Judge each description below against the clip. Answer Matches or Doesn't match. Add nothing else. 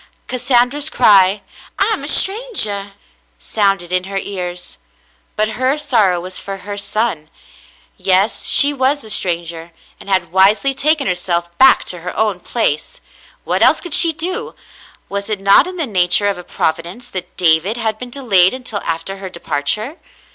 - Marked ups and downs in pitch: Matches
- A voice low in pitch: Doesn't match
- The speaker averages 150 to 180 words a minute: Matches